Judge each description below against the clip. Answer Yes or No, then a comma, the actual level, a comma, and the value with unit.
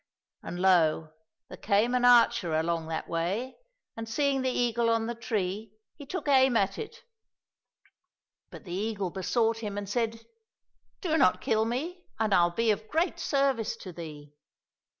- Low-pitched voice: No, high, 225 Hz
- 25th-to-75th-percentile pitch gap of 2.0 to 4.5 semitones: No, average, 5.2 semitones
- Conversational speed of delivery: Yes, average, 165 wpm